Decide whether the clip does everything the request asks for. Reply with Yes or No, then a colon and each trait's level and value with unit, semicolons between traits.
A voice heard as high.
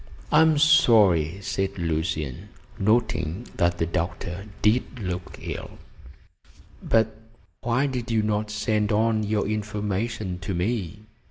No: low, 105 Hz